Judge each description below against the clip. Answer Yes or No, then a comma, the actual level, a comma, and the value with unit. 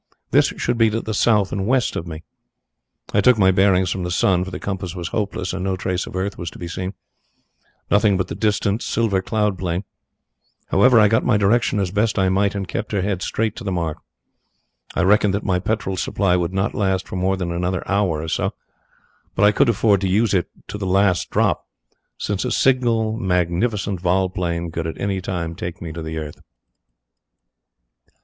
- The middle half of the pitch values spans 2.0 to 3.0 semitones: Yes, narrow, 2.6 semitones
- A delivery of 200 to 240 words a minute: Yes, fast, 205 wpm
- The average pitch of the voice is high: No, very low, 95 Hz